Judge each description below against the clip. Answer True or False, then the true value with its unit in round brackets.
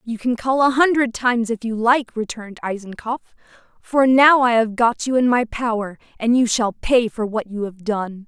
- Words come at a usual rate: False (210 wpm)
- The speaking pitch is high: True (235 Hz)